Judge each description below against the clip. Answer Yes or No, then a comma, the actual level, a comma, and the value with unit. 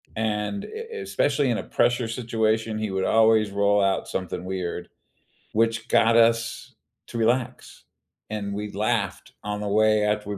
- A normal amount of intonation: No, narrow, 2.1 semitones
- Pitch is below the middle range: Yes, low, 110 Hz